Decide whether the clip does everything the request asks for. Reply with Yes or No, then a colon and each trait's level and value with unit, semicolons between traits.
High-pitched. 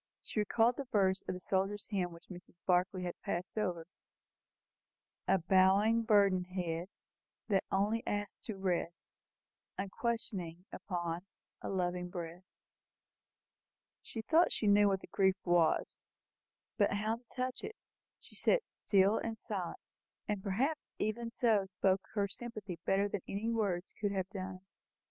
Yes: high, 195 Hz